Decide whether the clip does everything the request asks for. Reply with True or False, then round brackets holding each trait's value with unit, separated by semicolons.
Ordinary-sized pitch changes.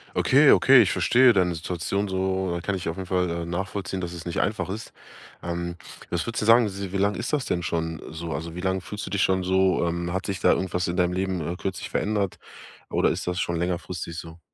False (2.0 semitones)